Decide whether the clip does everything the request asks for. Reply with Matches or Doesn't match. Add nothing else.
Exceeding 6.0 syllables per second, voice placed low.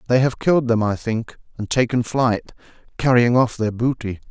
Doesn't match